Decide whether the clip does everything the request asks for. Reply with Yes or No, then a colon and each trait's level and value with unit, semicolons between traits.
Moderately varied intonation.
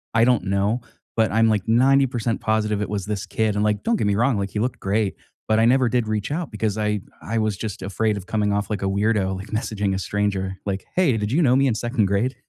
No: narrow, 2.3 semitones